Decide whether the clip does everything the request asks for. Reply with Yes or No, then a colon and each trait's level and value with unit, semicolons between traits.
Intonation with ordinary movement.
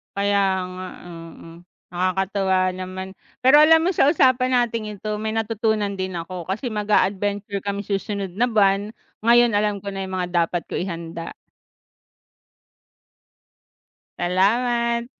Yes: average, 3.4 semitones